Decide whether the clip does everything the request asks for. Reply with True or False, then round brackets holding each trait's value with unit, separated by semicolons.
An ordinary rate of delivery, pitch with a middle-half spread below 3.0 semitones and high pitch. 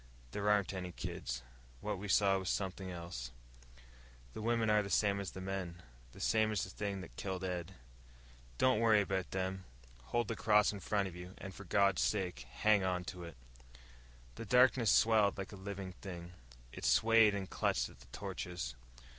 False (180 wpm; 2.4 semitones; 95 Hz)